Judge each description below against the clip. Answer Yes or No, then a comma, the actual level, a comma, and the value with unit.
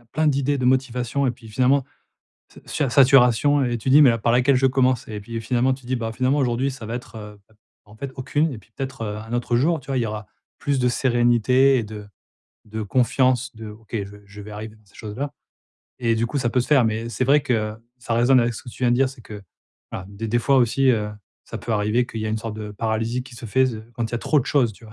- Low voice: Yes, low, 120 Hz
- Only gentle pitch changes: No, average, 3.1 semitones